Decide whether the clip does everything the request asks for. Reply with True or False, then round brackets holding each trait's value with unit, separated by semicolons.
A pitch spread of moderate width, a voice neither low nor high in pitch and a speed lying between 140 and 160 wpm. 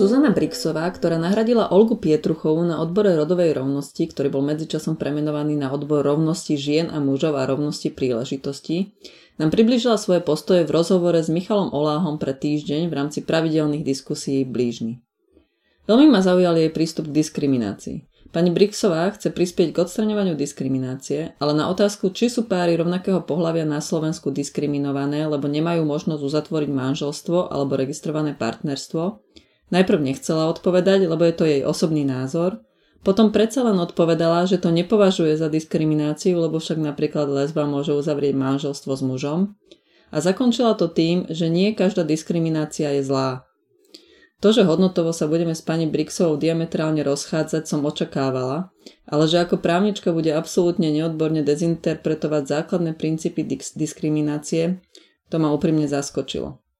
True (3.3 semitones; 160 Hz; 145 wpm)